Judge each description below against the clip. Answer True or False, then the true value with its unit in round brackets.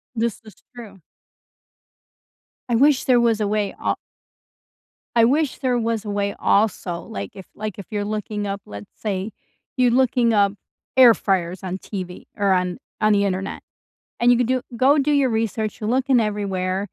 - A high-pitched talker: True (215 Hz)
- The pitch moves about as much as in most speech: True (3.5 semitones)